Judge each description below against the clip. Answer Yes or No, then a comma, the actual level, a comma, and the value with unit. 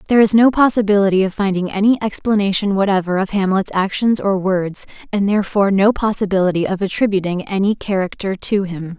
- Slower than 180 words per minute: Yes, average, 160 wpm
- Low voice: No, high, 195 Hz